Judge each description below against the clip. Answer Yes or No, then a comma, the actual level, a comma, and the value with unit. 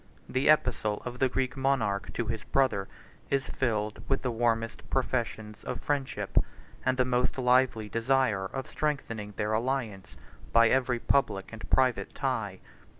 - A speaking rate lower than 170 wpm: Yes, average, 150 wpm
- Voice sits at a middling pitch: No, low, 125 Hz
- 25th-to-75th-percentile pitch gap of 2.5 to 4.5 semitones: Yes, average, 3.5 semitones